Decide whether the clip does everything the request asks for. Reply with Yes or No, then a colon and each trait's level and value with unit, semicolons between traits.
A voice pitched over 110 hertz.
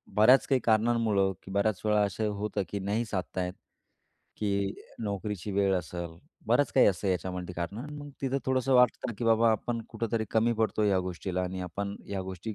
No: low, 105 Hz